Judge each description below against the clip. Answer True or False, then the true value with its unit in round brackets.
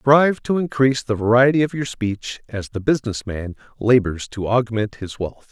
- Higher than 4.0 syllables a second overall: True (5.1 syllables/s)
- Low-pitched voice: True (120 Hz)